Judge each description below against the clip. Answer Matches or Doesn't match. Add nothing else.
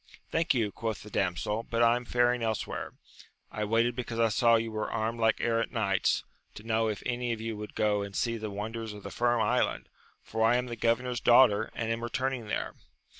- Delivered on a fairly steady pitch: Matches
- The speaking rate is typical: Doesn't match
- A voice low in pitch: Matches